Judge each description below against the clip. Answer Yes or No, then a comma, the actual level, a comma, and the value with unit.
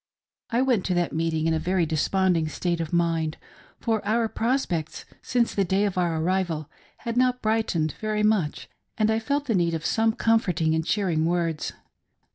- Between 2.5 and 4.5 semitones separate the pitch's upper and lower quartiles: No, average, 5.3 semitones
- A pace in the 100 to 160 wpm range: No, average, 185 wpm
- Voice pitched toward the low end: No, medium, 185 Hz